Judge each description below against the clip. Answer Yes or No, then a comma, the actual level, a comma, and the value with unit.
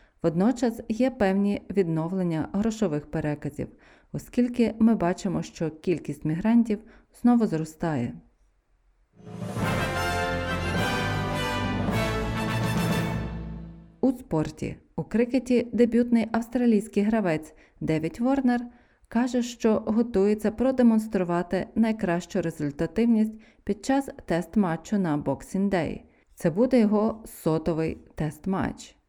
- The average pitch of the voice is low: No, high, 190 Hz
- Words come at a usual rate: No, slow, 85 wpm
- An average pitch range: No, wide, 6.4 semitones